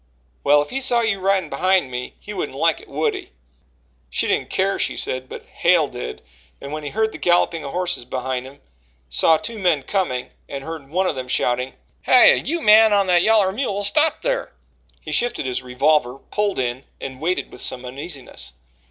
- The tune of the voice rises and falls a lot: Yes, wide, 7.4 semitones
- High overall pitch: No, medium, 160 Hz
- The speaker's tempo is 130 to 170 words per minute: No, average, 195 wpm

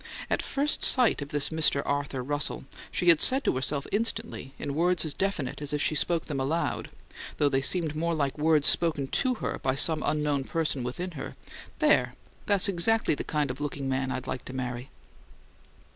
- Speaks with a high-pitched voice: No, medium, 150 Hz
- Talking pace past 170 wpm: Yes, average, 190 wpm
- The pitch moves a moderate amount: Yes, average, 3.9 semitones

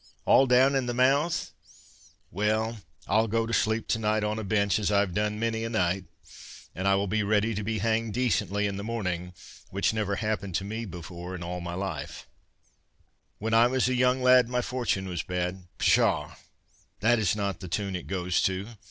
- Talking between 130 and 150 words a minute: No, average, 190 wpm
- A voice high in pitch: No, low, 105 Hz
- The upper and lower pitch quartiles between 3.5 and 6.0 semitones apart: No, average, 3.1 semitones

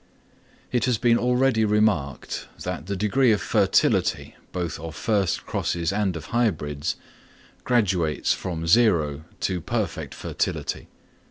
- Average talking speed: No, slow, 120 wpm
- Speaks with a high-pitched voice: No, very low, 95 Hz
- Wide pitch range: Yes, wide, 5.7 semitones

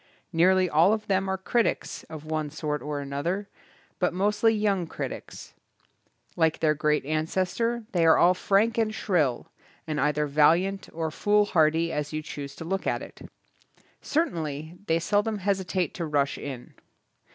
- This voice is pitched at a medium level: Yes, medium, 170 Hz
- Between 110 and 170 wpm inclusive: Yes, average, 155 wpm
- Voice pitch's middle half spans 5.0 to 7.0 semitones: No, average, 4.5 semitones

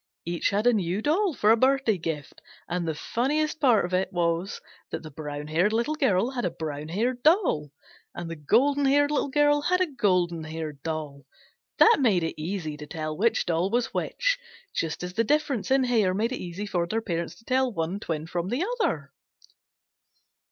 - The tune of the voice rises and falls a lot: Yes, wide, 7.9 semitones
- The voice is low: No, high, 195 Hz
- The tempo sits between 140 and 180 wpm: No, average, 195 wpm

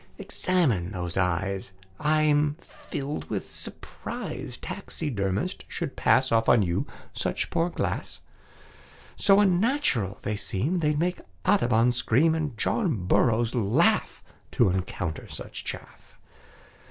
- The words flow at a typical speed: No, slow, 115 wpm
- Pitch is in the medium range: No, low, 125 Hz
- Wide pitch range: Yes, wide, 8.6 semitones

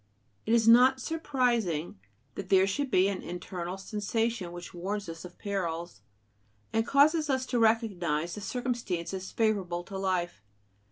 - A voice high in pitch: Yes, high, 200 Hz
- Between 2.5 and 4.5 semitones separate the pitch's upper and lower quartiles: No, average, 5.0 semitones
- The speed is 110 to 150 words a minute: Yes, average, 145 wpm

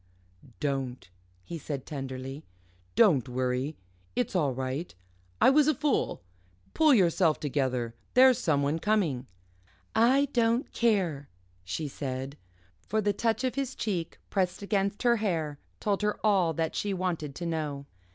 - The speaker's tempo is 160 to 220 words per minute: No, average, 140 wpm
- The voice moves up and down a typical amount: No, wide, 7.4 semitones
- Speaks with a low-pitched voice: No, medium, 165 Hz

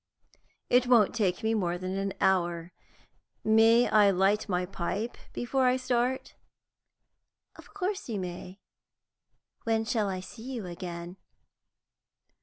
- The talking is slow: Yes, slow, 125 wpm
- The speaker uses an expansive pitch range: No, average, 4.6 semitones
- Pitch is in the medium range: No, high, 210 Hz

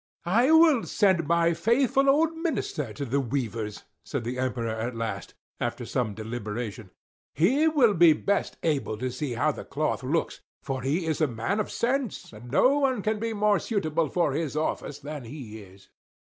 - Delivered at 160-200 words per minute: Yes, average, 180 wpm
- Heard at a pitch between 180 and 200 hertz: No, medium, 155 Hz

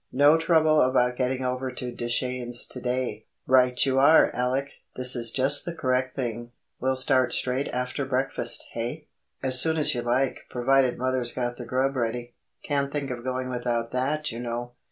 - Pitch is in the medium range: No, low, 130 Hz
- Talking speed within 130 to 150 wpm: No, average, 175 wpm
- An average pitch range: No, narrow, 1.7 semitones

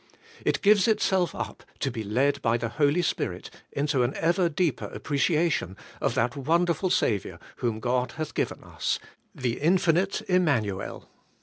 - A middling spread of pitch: No, wide, 6.2 semitones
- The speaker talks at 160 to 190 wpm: No, average, 150 wpm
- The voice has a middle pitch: Yes, medium, 145 Hz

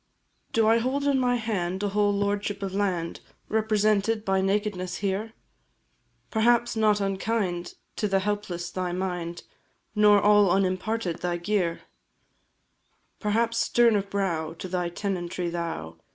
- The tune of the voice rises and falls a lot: No, average, 3.2 semitones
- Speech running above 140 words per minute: No, slow, 135 wpm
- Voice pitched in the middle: No, high, 200 Hz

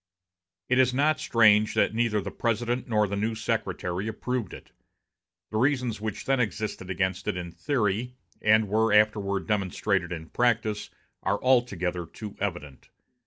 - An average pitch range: Yes, average, 3.4 semitones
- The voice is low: Yes, low, 105 Hz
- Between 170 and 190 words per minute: No, average, 150 wpm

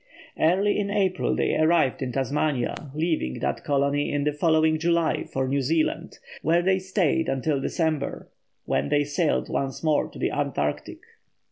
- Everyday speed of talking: Yes, average, 155 wpm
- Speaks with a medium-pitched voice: Yes, medium, 150 Hz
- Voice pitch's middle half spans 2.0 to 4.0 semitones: Yes, average, 3.4 semitones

